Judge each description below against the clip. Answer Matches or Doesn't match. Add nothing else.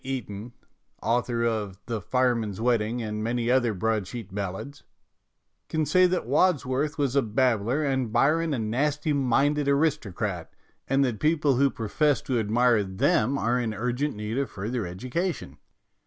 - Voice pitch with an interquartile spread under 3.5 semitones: Doesn't match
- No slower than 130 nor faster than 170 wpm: Matches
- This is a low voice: Matches